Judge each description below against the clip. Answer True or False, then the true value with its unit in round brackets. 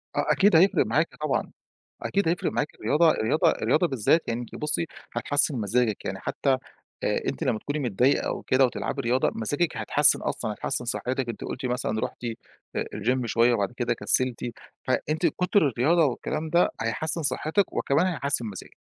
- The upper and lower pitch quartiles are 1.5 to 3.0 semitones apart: False (4.9 semitones)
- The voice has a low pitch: True (130 Hz)